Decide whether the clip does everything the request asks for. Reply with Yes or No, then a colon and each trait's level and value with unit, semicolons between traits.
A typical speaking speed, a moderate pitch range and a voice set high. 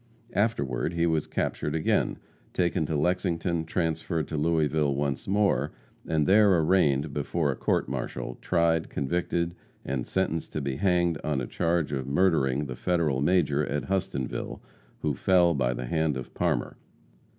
No: average, 150 wpm; average, 3.6 semitones; very low, 80 Hz